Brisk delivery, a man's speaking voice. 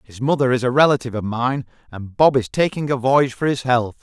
Yes: fast, 240 wpm; male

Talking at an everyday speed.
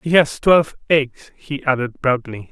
Yes: average, 165 wpm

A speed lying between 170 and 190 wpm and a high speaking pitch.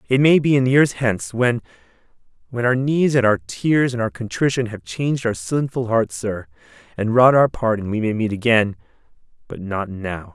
No: average, 180 wpm; low, 115 Hz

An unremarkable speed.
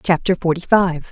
Yes: average, 160 wpm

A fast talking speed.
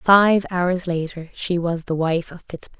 No: average, 195 wpm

